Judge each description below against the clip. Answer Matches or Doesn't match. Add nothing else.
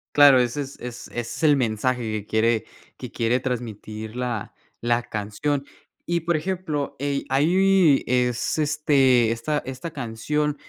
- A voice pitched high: Doesn't match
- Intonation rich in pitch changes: Doesn't match